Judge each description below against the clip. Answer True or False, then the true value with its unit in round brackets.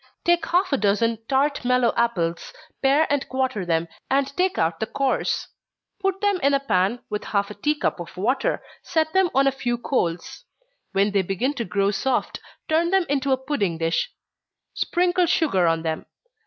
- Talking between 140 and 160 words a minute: False (185 wpm)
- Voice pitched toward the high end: True (260 Hz)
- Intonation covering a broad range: True (7.0 semitones)